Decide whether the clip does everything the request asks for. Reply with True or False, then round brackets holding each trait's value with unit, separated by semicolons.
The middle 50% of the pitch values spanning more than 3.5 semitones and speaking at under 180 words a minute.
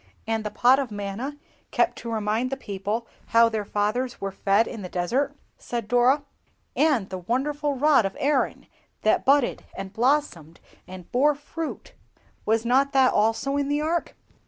True (5.1 semitones; 165 wpm)